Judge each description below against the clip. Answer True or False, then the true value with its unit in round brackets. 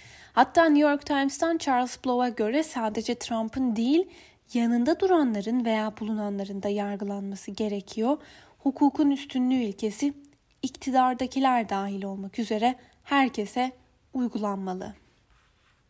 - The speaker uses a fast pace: False (100 wpm)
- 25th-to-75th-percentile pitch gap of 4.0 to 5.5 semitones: True (4.4 semitones)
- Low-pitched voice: False (245 Hz)